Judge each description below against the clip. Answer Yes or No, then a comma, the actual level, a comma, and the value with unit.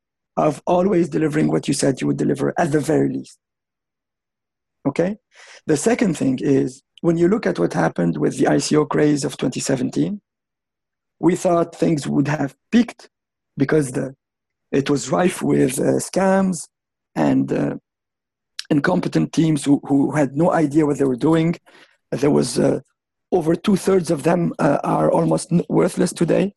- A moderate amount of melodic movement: Yes, average, 4.4 semitones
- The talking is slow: No, average, 160 wpm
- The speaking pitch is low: No, medium, 155 Hz